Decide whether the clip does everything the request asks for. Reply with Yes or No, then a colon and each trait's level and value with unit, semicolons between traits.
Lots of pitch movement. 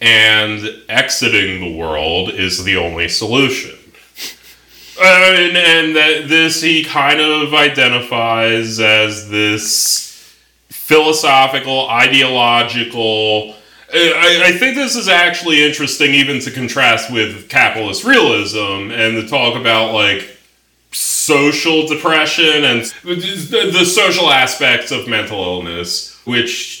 Yes: wide, 6.3 semitones